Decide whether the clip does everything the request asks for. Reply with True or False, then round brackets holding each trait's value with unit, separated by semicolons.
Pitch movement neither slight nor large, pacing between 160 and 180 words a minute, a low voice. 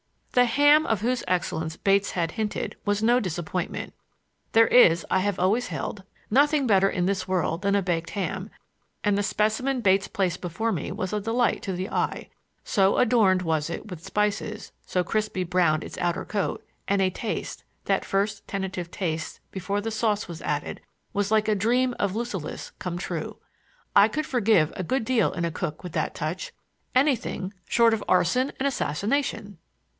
False (3.9 semitones; 170 wpm; 200 Hz)